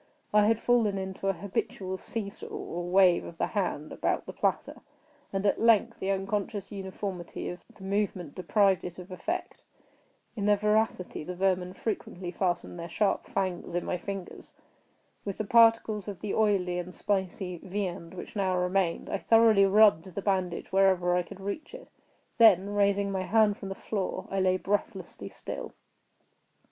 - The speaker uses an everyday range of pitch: No, narrow, 2.3 semitones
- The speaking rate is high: No, average, 170 wpm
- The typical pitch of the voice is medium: No, high, 195 Hz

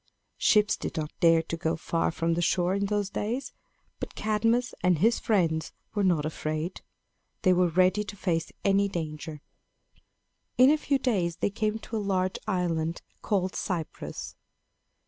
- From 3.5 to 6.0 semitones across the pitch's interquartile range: Yes, average, 4.0 semitones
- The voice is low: No, medium, 185 Hz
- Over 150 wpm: Yes, average, 160 wpm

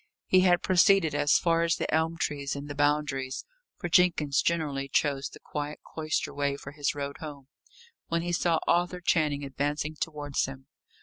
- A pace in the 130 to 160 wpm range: No, average, 175 wpm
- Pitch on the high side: No, medium, 150 Hz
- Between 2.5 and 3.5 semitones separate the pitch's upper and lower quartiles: Yes, average, 2.8 semitones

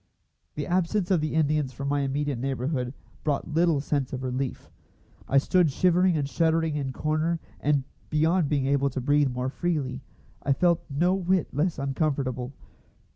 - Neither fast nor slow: Yes, average, 165 wpm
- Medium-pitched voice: Yes, medium, 145 Hz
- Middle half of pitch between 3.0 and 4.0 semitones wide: Yes, average, 3.4 semitones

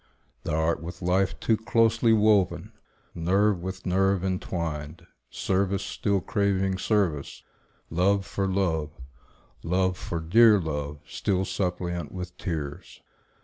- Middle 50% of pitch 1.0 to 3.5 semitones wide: Yes, average, 3.0 semitones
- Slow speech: Yes, slow, 115 wpm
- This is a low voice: Yes, very low, 95 Hz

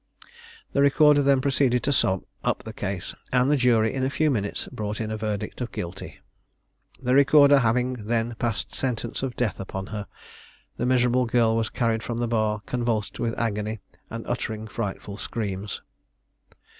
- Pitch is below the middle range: Yes, low, 115 Hz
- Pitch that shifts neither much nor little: Yes, average, 3.0 semitones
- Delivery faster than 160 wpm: Yes, average, 170 wpm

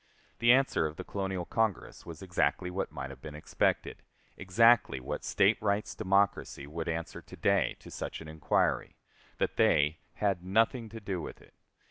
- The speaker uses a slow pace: No, average, 170 wpm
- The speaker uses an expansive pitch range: No, average, 4.9 semitones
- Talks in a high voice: No, very low, 95 Hz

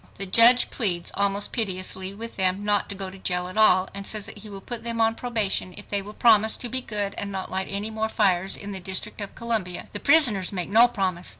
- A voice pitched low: No, high, 200 Hz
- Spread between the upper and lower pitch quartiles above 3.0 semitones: No, average, 2.7 semitones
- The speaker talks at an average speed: No, fast, 240 wpm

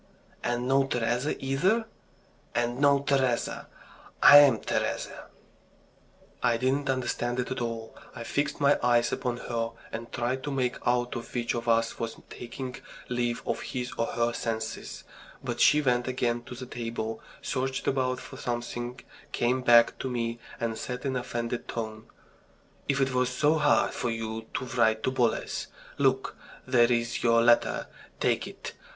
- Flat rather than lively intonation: Yes, narrow, 1.9 semitones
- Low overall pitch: Yes, low, 120 Hz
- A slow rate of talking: No, average, 155 wpm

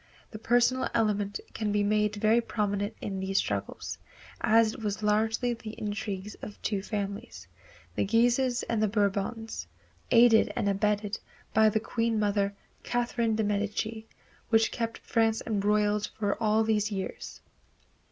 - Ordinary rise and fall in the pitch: No, narrow, 1.7 semitones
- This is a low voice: No, high, 215 Hz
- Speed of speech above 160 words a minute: No, average, 140 wpm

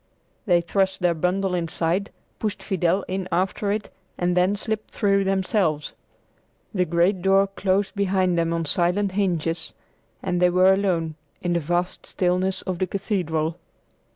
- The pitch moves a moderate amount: No, narrow, 2.1 semitones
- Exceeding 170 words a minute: No, average, 150 wpm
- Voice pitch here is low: No, medium, 185 Hz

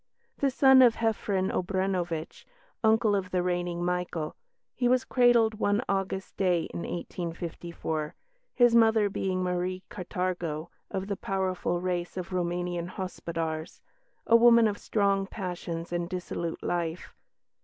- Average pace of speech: No, slow, 130 wpm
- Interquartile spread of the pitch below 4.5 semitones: Yes, average, 2.9 semitones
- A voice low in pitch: No, medium, 185 Hz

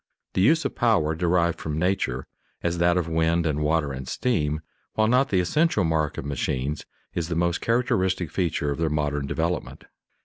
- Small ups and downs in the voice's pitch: No, average, 3.5 semitones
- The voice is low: Yes, very low, 85 Hz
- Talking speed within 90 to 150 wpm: No, average, 180 wpm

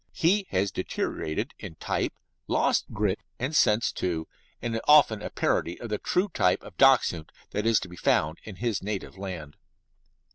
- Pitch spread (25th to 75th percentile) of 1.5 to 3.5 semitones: No, average, 4.6 semitones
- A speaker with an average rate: Yes, average, 175 wpm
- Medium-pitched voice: No, low, 105 Hz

